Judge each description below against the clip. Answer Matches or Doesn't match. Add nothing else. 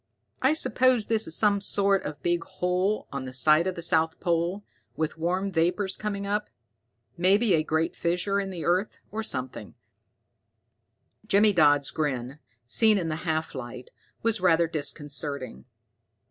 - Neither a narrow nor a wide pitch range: Matches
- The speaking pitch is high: Doesn't match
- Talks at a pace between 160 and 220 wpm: Doesn't match